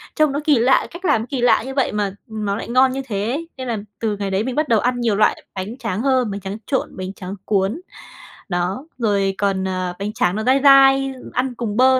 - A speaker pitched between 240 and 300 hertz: No, high, 225 Hz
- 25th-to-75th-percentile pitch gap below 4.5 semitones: No, average, 4.8 semitones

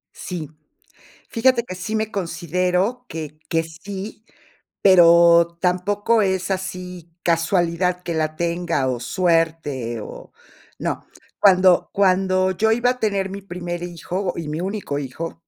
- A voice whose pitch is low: No, medium, 180 Hz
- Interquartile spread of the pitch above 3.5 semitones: No, narrow, 2.6 semitones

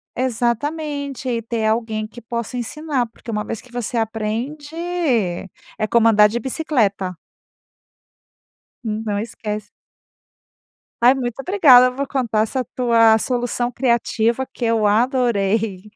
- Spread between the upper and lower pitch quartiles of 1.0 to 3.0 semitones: Yes, average, 2.7 semitones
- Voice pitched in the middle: No, high, 235 Hz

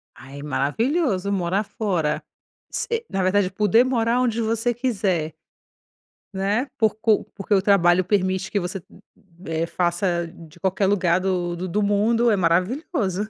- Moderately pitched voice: No, high, 195 Hz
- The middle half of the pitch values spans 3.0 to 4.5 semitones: Yes, average, 3.8 semitones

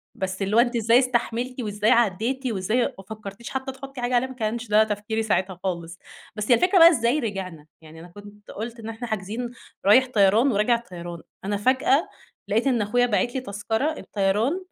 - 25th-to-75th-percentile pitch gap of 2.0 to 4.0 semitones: Yes, average, 3.6 semitones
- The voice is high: Yes, high, 225 Hz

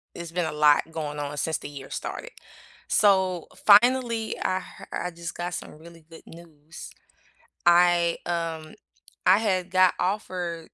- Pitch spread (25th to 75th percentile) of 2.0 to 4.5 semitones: Yes, narrow, 2.6 semitones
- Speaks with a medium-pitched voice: Yes, medium, 170 Hz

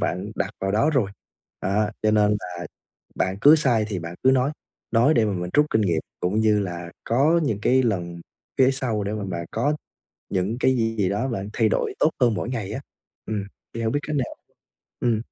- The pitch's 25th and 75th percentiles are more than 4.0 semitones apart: Yes, average, 4.6 semitones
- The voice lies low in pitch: Yes, low, 110 Hz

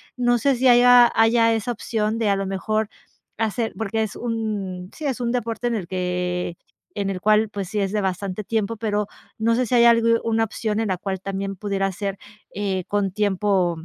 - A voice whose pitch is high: Yes, high, 210 Hz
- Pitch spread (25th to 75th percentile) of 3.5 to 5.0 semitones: No, average, 2.8 semitones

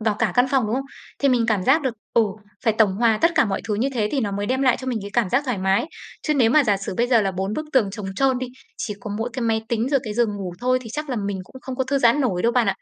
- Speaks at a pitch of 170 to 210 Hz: No, high, 235 Hz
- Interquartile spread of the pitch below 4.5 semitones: Yes, average, 3.9 semitones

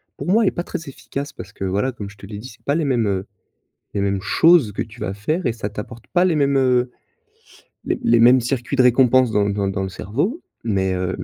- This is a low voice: Yes, low, 120 Hz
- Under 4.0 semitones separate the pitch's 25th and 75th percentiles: No, wide, 5.4 semitones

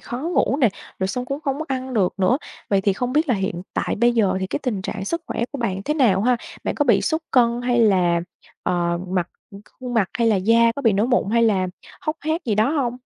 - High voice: Yes, high, 235 Hz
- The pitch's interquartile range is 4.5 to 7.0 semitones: Yes, average, 5.0 semitones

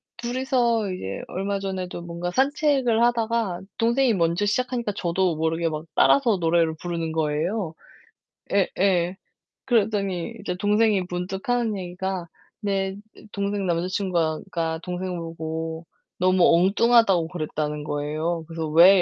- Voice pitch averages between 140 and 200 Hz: Yes, medium, 185 Hz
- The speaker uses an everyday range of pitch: Yes, average, 4.0 semitones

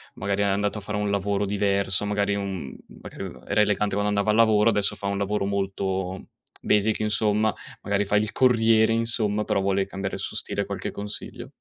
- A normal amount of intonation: No, narrow, 1.2 semitones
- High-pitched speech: No, low, 100 Hz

